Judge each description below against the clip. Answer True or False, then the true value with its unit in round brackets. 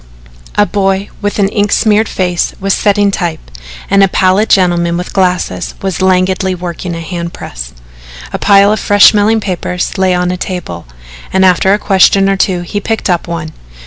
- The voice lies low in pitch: False (190 Hz)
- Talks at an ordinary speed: True (180 wpm)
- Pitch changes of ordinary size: False (2.3 semitones)